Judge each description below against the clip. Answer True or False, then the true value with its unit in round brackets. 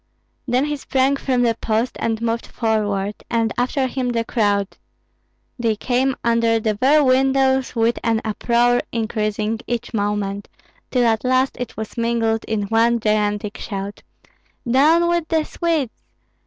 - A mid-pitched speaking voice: False (230 Hz)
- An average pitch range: True (3.0 semitones)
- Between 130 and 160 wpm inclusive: True (145 wpm)